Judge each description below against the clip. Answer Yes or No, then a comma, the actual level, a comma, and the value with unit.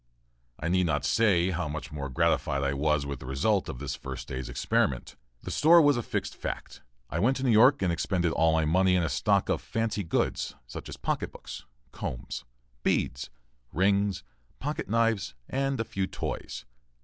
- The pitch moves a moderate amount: No, wide, 7.8 semitones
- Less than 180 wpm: No, average, 185 wpm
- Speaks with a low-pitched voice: Yes, very low, 85 Hz